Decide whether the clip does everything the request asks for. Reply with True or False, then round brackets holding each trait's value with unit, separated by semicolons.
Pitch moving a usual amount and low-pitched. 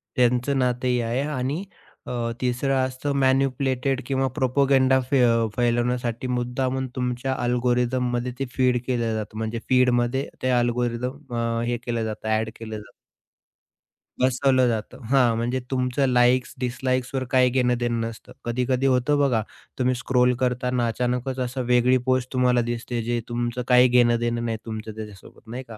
False (1.4 semitones; 125 Hz)